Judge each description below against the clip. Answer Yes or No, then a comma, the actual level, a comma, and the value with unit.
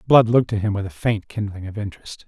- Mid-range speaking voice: No, low, 105 Hz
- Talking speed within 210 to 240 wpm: No, fast, 265 wpm